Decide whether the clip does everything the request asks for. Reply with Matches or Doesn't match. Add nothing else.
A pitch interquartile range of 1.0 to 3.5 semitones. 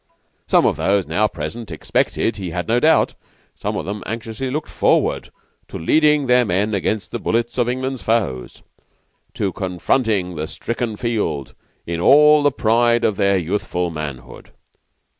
Doesn't match